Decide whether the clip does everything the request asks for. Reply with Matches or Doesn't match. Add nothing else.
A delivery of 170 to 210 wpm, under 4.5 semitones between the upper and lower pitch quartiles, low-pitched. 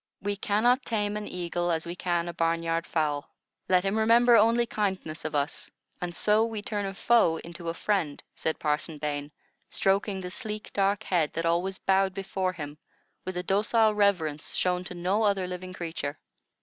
Doesn't match